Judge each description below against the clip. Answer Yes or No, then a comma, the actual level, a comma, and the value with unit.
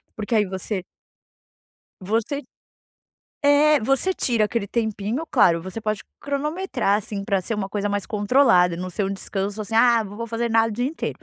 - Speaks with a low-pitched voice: No, high, 215 Hz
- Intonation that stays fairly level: No, average, 3.6 semitones